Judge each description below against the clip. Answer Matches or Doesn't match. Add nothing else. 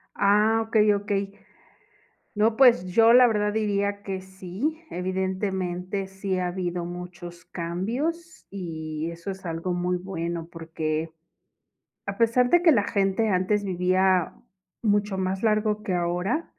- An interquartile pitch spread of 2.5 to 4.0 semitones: Matches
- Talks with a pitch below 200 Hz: Matches